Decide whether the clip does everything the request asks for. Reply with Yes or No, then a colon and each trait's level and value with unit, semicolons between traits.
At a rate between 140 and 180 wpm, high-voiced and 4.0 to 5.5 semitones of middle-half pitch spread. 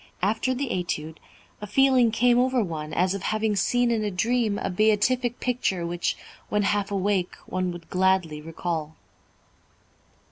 Yes: average, 150 wpm; high, 205 Hz; average, 5.0 semitones